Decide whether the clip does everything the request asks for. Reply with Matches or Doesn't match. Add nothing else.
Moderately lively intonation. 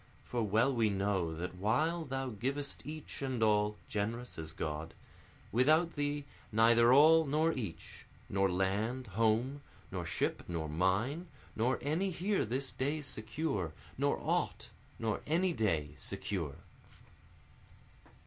Doesn't match